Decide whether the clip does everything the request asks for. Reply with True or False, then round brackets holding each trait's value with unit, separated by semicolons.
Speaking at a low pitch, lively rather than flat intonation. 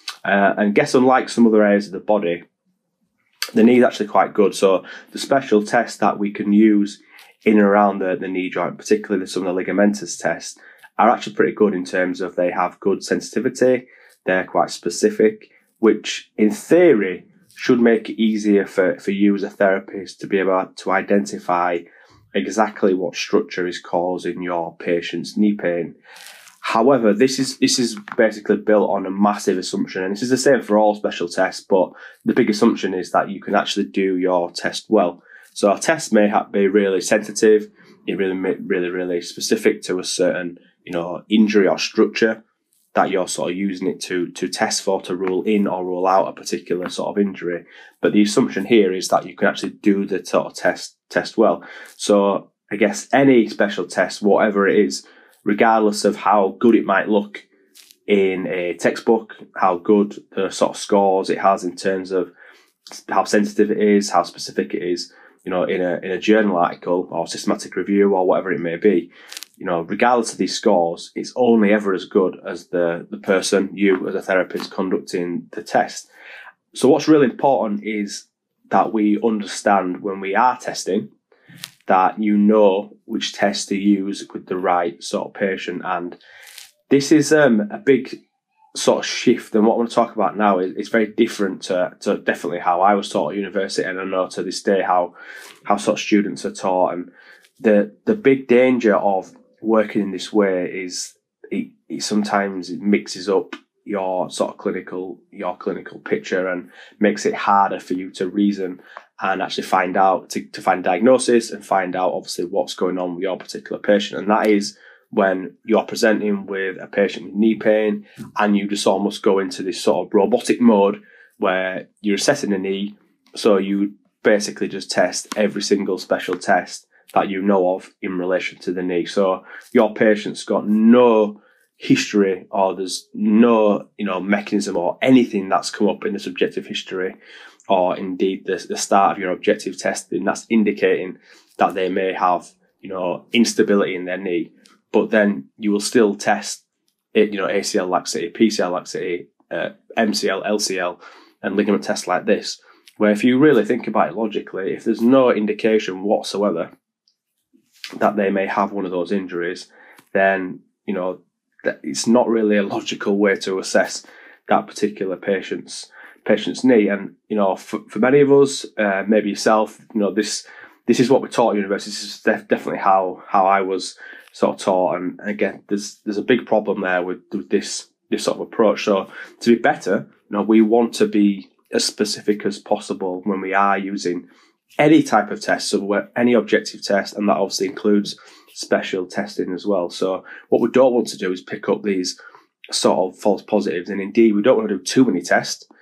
False (100 Hz; 2.5 semitones)